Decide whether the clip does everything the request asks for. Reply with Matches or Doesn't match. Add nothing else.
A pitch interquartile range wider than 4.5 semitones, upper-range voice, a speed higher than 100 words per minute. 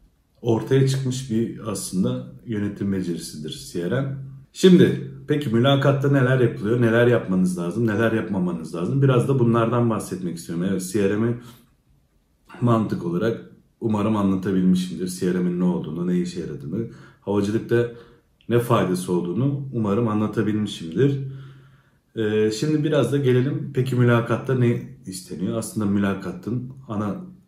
Doesn't match